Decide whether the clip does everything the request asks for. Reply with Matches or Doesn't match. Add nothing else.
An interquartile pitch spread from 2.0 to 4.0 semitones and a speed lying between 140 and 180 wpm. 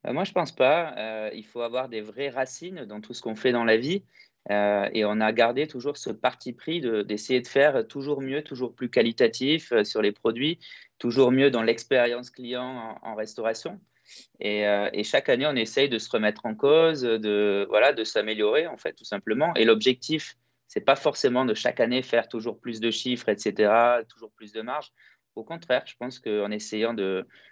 Doesn't match